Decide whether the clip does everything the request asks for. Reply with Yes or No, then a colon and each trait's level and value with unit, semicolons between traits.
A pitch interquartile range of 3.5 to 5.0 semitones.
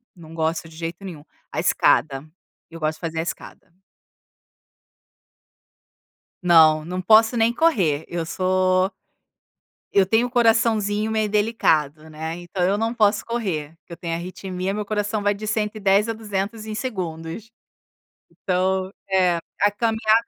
Yes: average, 4.6 semitones